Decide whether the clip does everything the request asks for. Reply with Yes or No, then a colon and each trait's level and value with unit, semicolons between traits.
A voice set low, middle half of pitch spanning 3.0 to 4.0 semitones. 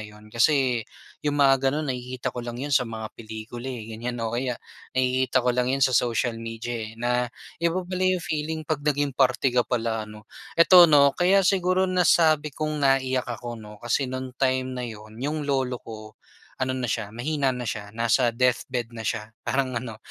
Yes: low, 125 Hz; average, 3.4 semitones